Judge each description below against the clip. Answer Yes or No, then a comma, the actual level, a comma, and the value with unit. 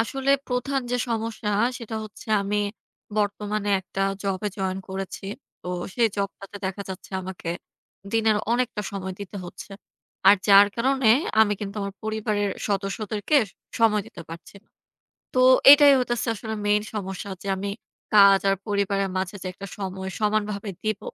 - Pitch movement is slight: Yes, narrow, 2.1 semitones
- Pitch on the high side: Yes, high, 205 Hz